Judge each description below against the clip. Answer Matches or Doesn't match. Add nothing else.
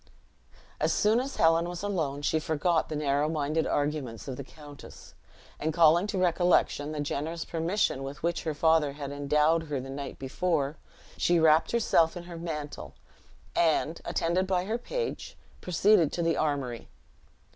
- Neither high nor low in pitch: Matches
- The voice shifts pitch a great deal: Doesn't match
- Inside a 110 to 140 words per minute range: Doesn't match